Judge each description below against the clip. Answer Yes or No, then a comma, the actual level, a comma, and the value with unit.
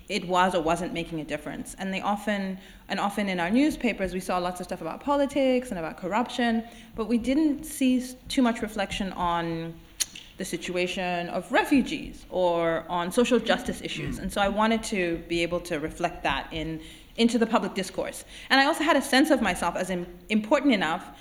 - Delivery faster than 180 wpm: Yes, average, 190 wpm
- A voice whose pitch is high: Yes, high, 195 Hz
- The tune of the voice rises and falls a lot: Yes, wide, 5.8 semitones